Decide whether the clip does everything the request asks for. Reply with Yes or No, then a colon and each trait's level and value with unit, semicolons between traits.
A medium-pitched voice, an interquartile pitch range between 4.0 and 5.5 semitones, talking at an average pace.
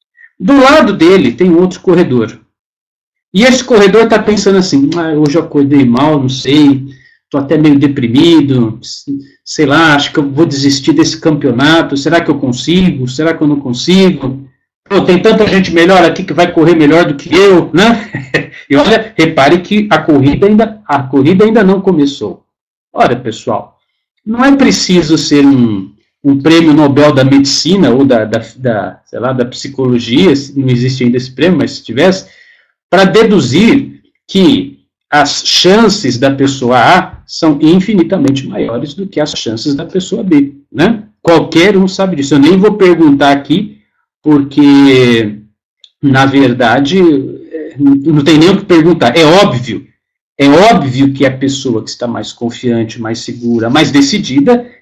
Yes: medium, 155 Hz; average, 5.2 semitones; average, 165 wpm